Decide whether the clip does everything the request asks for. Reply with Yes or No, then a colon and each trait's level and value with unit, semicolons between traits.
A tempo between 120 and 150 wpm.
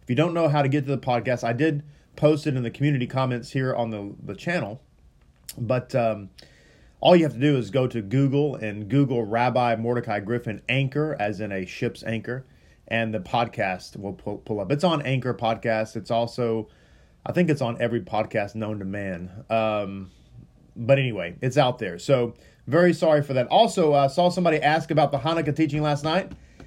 No: average, 200 wpm